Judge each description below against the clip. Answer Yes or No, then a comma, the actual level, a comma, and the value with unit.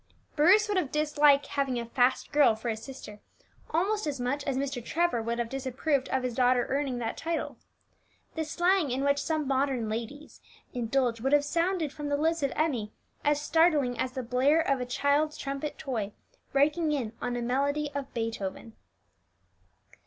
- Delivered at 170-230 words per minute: Yes, average, 180 wpm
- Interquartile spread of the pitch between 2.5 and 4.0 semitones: Yes, average, 3.5 semitones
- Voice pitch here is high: Yes, very high, 275 Hz